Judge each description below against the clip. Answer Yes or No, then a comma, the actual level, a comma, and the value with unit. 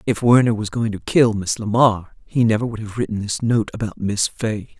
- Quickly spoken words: Yes, fast, 225 wpm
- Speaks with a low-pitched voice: Yes, low, 110 Hz